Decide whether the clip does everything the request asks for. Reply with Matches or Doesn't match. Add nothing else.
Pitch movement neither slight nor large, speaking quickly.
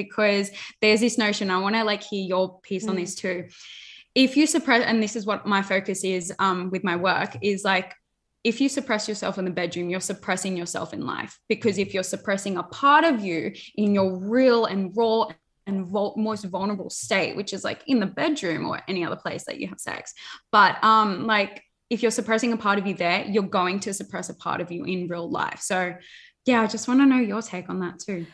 Matches